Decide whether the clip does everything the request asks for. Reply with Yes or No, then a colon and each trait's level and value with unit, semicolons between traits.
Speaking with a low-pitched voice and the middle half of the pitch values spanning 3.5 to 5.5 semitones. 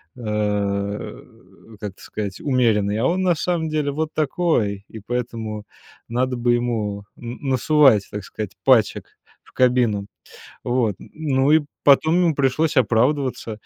Yes: low, 120 Hz; average, 5.2 semitones